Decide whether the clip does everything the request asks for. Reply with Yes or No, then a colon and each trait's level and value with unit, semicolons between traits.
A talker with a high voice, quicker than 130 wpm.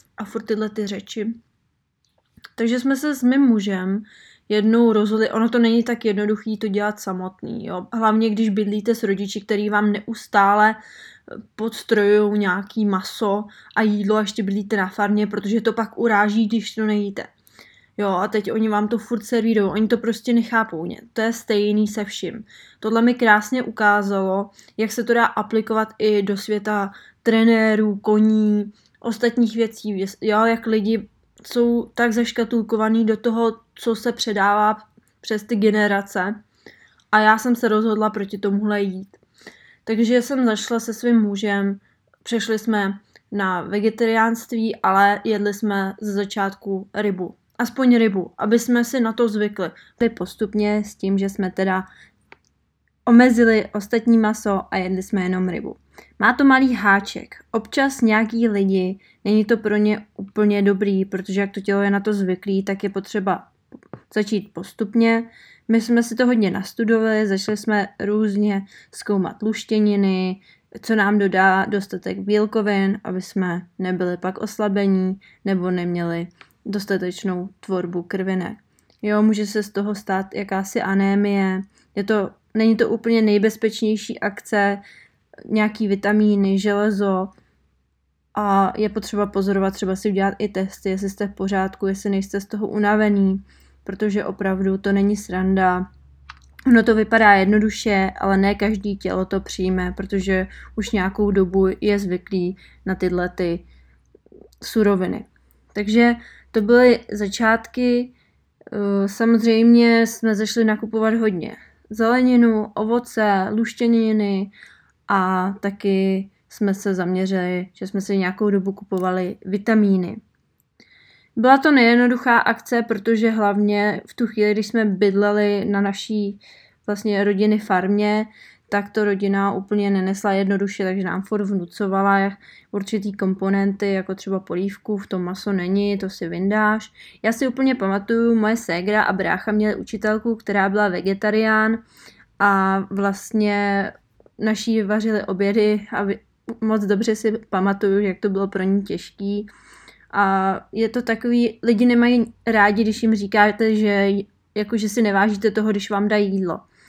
Yes: high, 210 Hz; average, 140 wpm